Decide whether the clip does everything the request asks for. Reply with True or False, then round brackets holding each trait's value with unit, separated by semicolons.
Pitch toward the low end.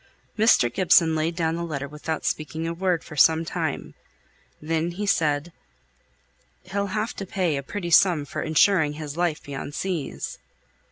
False (165 Hz)